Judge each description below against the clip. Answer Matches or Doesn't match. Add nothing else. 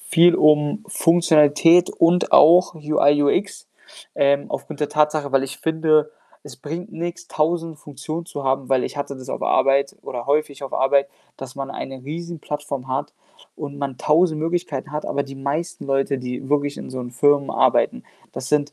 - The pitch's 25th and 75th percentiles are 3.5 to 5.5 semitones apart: Doesn't match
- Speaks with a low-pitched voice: Doesn't match